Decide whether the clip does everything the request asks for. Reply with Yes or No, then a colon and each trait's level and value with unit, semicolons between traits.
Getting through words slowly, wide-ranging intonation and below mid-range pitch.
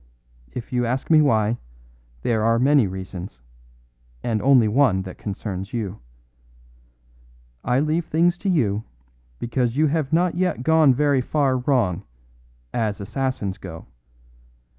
Yes: slow, 130 wpm; wide, 5.9 semitones; low, 125 Hz